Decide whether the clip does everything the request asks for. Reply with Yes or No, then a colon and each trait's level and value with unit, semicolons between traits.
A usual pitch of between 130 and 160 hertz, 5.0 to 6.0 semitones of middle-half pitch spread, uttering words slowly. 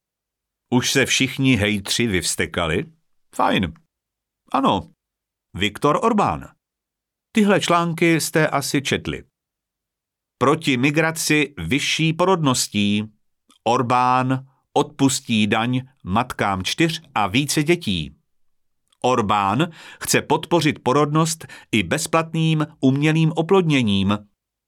Yes: medium, 140 Hz; average, 5.3 semitones; slow, 85 wpm